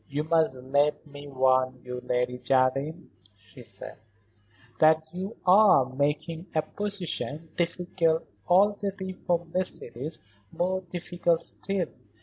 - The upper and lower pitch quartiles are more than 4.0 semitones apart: Yes, average, 5.2 semitones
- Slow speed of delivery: Yes, slow, 115 wpm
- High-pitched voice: No, medium, 160 Hz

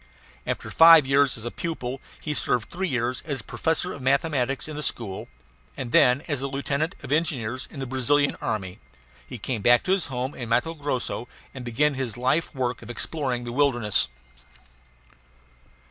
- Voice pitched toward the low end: Yes, low, 130 Hz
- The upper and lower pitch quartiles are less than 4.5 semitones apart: Yes, average, 3.3 semitones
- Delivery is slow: No, average, 170 wpm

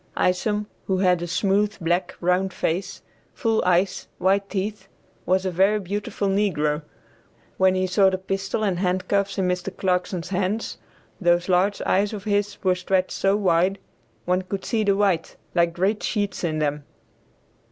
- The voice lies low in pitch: No, high, 190 Hz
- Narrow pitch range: Yes, narrow, 1.8 semitones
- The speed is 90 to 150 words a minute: No, average, 160 wpm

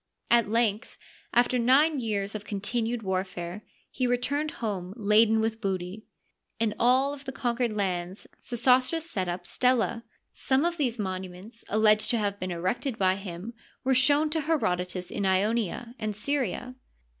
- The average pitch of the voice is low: No, high, 220 Hz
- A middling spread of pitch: Yes, average, 4.5 semitones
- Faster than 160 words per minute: No, average, 150 wpm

